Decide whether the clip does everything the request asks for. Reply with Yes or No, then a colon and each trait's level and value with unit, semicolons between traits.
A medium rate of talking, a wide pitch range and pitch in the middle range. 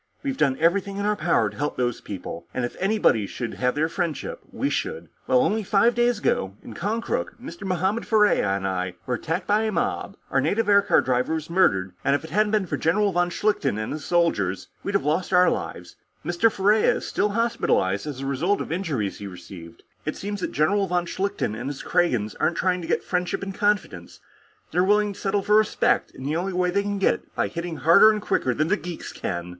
No: fast, 225 wpm; wide, 7.6 semitones; medium, 175 Hz